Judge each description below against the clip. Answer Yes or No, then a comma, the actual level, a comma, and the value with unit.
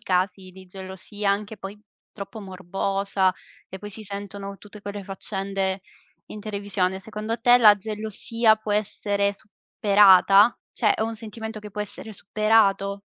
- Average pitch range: No, narrow, 1.7 semitones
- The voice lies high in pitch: Yes, high, 205 Hz